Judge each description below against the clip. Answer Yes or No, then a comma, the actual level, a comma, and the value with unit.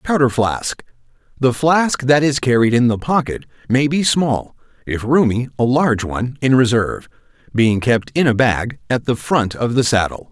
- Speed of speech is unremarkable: Yes, average, 175 wpm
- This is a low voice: Yes, low, 125 Hz